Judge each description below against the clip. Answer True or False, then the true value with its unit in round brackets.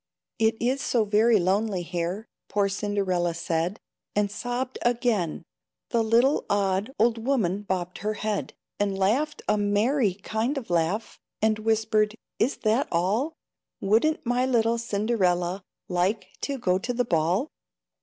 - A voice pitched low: False (215 Hz)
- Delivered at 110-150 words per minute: True (140 wpm)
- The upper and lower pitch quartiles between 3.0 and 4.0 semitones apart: True (3.7 semitones)